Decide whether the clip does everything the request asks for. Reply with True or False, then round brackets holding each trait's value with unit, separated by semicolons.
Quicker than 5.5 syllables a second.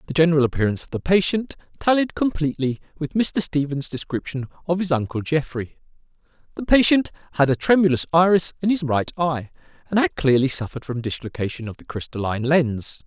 True (6.0 syllables/s)